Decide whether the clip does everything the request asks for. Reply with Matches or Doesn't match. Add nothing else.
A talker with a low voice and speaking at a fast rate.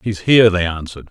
Matches